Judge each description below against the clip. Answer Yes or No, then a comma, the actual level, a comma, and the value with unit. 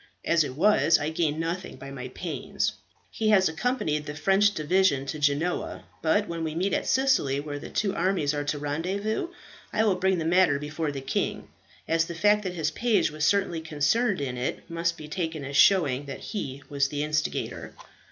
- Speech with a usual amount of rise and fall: Yes, average, 4.6 semitones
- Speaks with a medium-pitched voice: Yes, medium, 160 Hz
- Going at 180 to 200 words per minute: Yes, average, 195 wpm